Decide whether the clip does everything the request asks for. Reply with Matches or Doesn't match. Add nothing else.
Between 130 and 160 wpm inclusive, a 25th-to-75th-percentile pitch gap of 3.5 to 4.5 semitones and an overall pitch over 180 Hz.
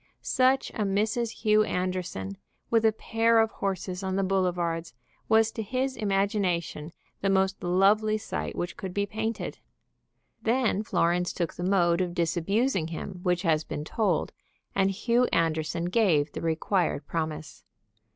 Matches